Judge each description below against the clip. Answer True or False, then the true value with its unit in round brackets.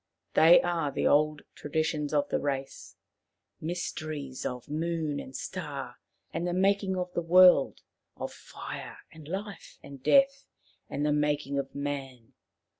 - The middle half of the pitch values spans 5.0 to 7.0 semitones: False (3.7 semitones)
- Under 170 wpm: True (150 wpm)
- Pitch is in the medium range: True (150 Hz)